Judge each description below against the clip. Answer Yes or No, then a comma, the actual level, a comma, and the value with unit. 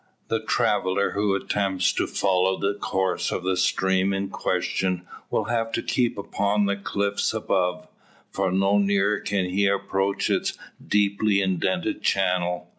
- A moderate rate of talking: Yes, average, 145 wpm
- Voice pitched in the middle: No, very low, 95 Hz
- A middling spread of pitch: No, narrow, 1.3 semitones